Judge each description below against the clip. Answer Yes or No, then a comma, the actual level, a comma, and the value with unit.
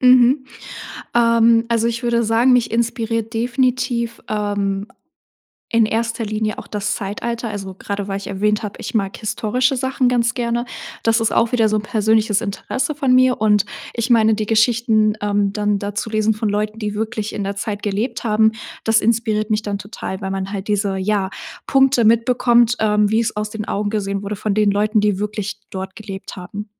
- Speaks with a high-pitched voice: Yes, high, 215 Hz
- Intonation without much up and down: Yes, narrow, 2.2 semitones